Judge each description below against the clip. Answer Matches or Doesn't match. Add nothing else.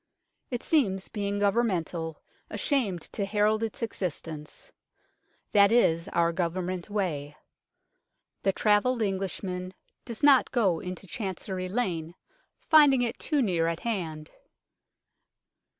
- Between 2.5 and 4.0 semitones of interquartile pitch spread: Doesn't match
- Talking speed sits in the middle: Doesn't match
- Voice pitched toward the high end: Matches